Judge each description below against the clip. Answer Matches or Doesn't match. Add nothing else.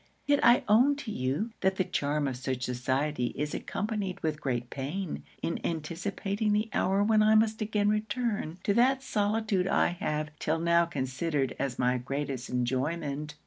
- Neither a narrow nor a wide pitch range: Doesn't match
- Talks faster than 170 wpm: Doesn't match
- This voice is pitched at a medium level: Matches